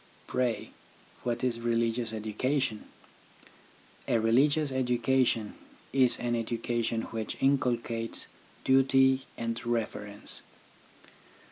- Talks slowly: Yes, slow, 85 wpm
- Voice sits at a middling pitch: No, low, 120 Hz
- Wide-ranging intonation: No, narrow, 2.4 semitones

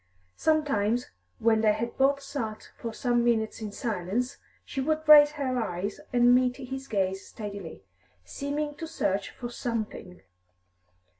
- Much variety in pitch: No, average, 4.5 semitones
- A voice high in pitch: Yes, high, 240 Hz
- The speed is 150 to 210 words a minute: No, average, 140 wpm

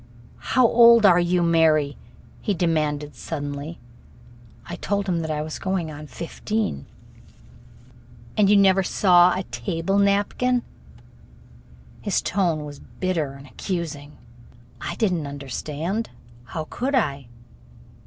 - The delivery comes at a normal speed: No, slow, 125 wpm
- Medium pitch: Yes, medium, 170 Hz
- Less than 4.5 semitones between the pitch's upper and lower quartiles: No, average, 4.9 semitones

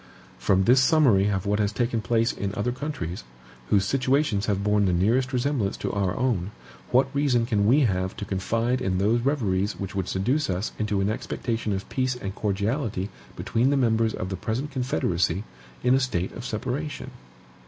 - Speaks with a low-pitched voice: Yes, low, 110 Hz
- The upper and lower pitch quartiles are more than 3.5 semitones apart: Yes, average, 4.7 semitones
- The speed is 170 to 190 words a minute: Yes, average, 185 wpm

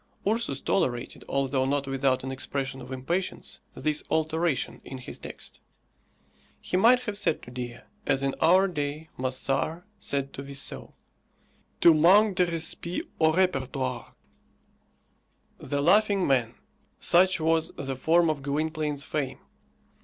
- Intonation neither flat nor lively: Yes, average, 4.3 semitones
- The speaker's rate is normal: No, slow, 130 wpm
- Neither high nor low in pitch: Yes, medium, 150 Hz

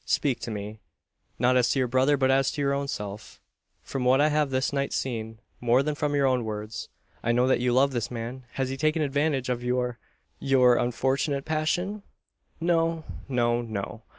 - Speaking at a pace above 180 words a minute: Yes, average, 195 wpm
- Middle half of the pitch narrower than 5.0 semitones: Yes, average, 2.8 semitones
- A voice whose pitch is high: No, low, 130 Hz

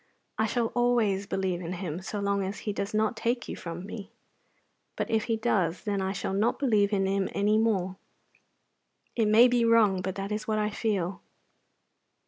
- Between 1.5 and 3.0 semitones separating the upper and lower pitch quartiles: Yes, narrow, 2.5 semitones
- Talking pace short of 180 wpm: No, average, 190 wpm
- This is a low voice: No, high, 205 Hz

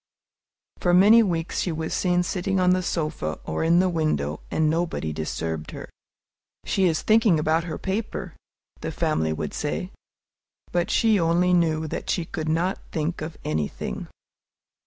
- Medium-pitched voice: Yes, medium, 165 Hz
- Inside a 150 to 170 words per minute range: Yes, average, 155 wpm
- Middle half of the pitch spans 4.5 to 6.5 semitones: No, average, 2.7 semitones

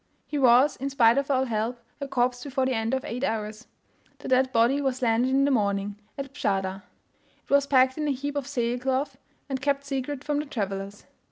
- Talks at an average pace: No, fast, 210 wpm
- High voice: Yes, very high, 260 Hz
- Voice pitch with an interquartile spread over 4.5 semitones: No, average, 3.2 semitones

